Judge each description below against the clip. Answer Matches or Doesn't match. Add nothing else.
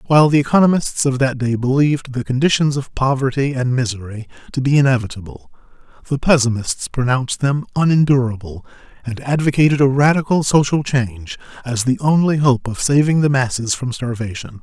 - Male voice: Matches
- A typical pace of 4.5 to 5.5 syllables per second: Doesn't match